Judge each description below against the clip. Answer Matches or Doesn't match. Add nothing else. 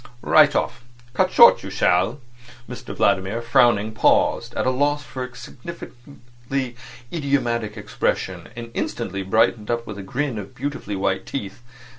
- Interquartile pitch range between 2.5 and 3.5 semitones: Doesn't match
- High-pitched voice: Doesn't match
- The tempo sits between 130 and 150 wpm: Matches